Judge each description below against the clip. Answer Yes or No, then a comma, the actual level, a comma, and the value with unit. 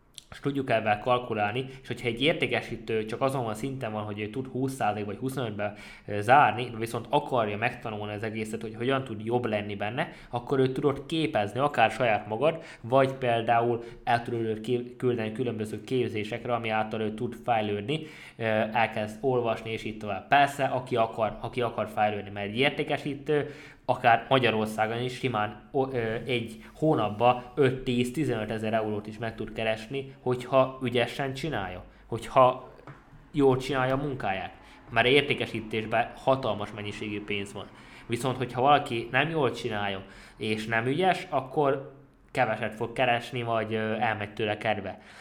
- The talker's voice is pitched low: Yes, low, 120 Hz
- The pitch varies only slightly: No, average, 3.4 semitones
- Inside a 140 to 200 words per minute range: Yes, average, 145 wpm